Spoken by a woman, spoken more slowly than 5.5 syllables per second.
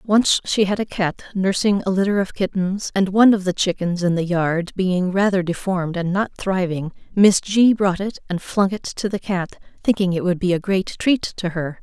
Yes: female; 4.9 syllables/s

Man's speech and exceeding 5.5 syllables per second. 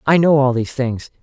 Yes: male; 5.9 syllables/s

